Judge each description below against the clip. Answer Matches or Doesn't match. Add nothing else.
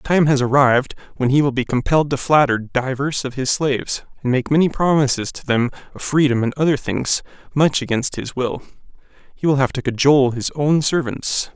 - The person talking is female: Doesn't match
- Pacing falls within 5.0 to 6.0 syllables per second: Matches